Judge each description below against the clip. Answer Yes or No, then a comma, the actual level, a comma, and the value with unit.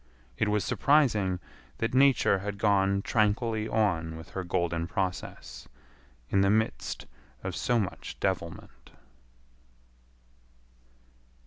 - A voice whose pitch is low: Yes, low, 100 Hz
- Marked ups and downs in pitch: No, average, 3.4 semitones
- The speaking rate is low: Yes, slow, 105 wpm